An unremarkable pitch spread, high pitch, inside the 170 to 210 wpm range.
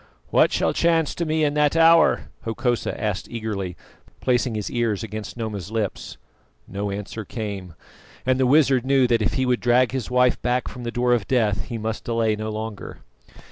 No: average, 3.1 semitones; low, 120 Hz; average, 185 wpm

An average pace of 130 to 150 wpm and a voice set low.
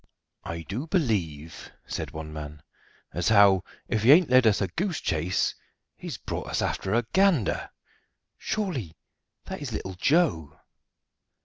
Yes: average, 140 wpm; low, 100 Hz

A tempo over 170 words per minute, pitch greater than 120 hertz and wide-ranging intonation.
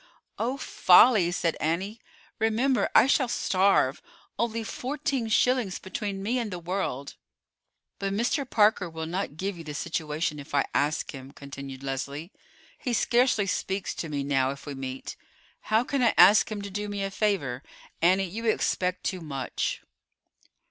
No: average, 160 wpm; high, 190 Hz; wide, 6.6 semitones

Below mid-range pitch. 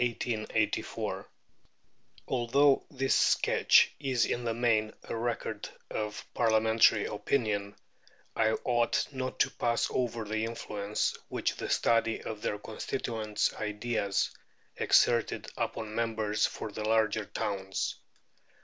Yes: low, 110 Hz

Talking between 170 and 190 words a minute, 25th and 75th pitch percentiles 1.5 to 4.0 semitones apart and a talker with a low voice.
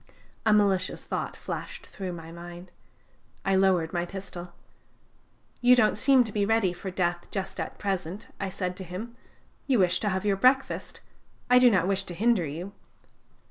No: average, 175 wpm; average, 3.0 semitones; high, 190 Hz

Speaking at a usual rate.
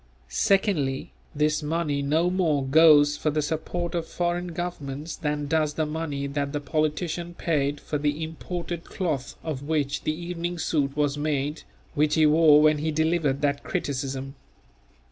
Yes: average, 155 wpm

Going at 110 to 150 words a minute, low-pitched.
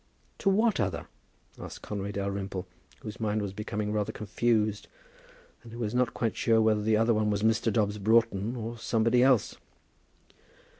No: average, 160 wpm; low, 110 Hz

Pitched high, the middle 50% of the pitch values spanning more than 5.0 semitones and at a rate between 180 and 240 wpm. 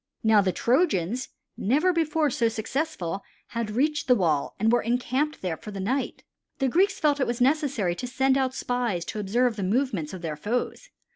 Yes: high, 245 Hz; wide, 5.4 semitones; average, 195 wpm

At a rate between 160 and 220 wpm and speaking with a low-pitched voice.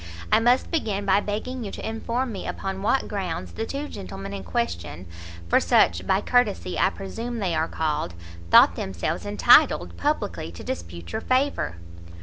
No: average, 165 wpm; high, 195 Hz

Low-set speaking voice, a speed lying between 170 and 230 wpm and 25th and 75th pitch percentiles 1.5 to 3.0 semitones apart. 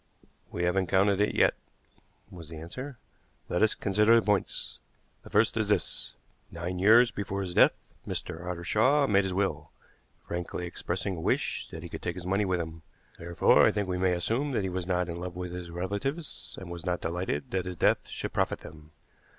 Yes: very low, 90 Hz; average, 200 wpm; average, 2.7 semitones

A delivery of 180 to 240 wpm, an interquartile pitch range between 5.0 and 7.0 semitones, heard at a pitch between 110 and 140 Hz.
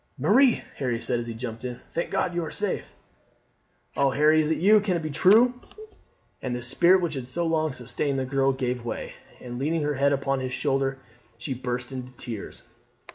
No: average, 200 wpm; average, 4.5 semitones; low, 135 Hz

